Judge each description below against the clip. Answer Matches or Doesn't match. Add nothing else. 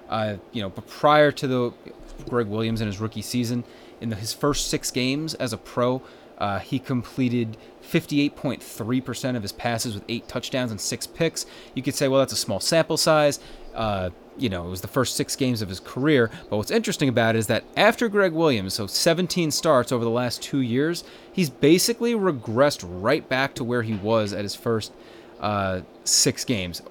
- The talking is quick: Doesn't match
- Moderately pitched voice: Doesn't match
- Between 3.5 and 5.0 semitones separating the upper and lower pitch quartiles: Matches